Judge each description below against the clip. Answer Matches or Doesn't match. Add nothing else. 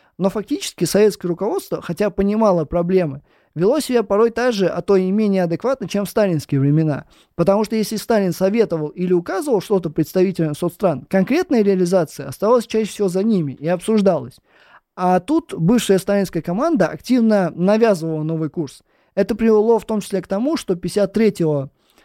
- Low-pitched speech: Doesn't match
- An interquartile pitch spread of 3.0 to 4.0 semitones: Matches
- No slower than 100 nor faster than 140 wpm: Doesn't match